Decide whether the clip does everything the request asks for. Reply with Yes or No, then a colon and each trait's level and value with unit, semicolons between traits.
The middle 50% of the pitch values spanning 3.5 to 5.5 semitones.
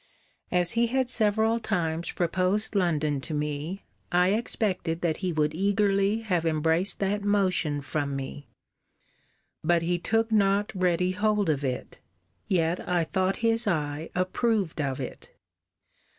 Yes: average, 4.3 semitones